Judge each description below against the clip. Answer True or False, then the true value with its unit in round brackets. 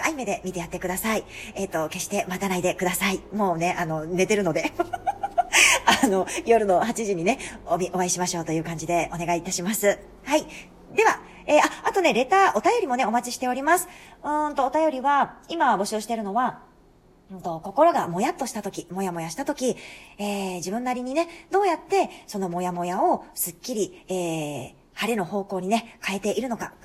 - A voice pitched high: True (205 Hz)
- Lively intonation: True (7.2 semitones)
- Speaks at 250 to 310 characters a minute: False (380 characters per minute)